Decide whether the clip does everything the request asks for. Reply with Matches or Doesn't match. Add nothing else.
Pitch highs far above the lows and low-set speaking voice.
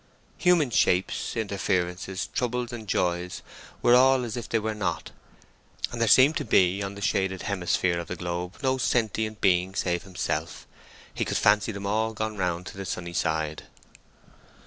Doesn't match